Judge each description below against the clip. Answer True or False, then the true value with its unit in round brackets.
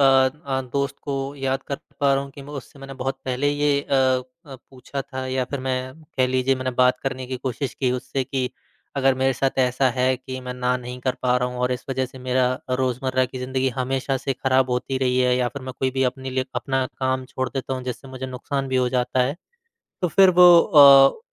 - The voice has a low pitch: True (130 Hz)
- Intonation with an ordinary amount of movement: False (1.1 semitones)